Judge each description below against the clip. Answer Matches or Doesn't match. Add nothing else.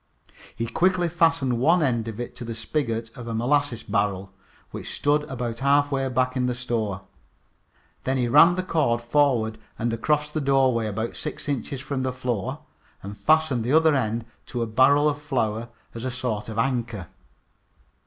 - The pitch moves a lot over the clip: Doesn't match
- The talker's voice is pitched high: Doesn't match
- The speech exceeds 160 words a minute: Matches